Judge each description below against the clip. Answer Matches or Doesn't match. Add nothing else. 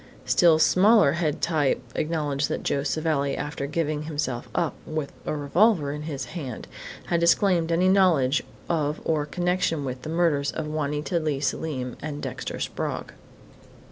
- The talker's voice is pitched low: Doesn't match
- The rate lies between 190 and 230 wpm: Doesn't match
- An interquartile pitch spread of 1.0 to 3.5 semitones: Matches